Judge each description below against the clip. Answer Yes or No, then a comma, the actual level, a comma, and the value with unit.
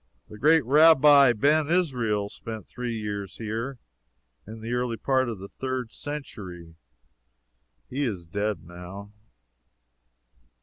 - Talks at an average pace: No, slow, 120 wpm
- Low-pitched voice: Yes, low, 115 Hz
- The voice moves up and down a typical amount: Yes, average, 5.0 semitones